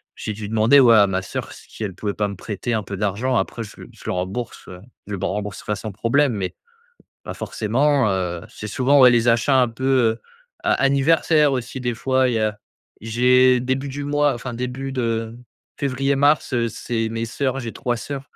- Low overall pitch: Yes, low, 120 Hz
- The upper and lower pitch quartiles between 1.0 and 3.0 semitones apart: No, average, 3.7 semitones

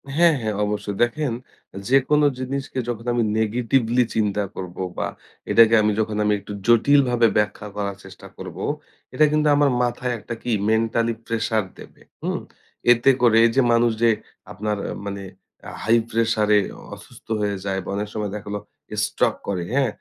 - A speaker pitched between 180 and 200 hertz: No, low, 115 Hz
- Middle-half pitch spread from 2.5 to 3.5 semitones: Yes, average, 2.9 semitones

